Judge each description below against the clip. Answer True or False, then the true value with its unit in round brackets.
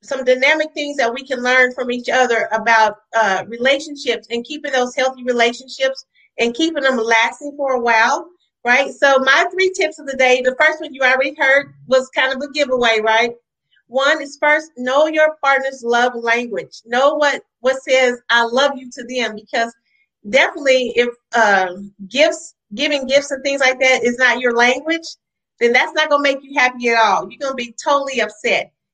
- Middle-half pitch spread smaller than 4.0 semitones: True (3.1 semitones)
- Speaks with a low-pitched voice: False (260 Hz)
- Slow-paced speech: False (190 wpm)